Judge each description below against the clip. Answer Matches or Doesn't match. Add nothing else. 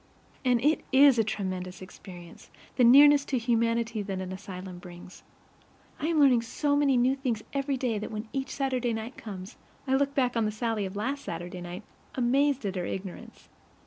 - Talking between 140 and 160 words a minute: Doesn't match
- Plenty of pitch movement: Matches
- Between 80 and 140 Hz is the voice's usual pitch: Doesn't match